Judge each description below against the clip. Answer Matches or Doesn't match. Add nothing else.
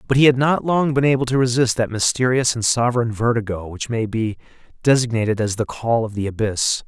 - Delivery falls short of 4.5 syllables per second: Doesn't match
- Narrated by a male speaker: Matches